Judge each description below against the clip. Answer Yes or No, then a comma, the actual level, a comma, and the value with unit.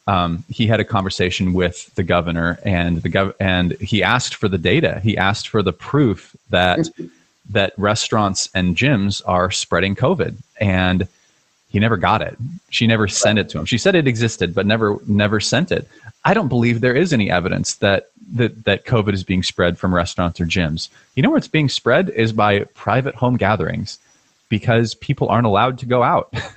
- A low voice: Yes, low, 105 Hz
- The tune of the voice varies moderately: Yes, average, 3.8 semitones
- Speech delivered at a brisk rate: No, average, 195 wpm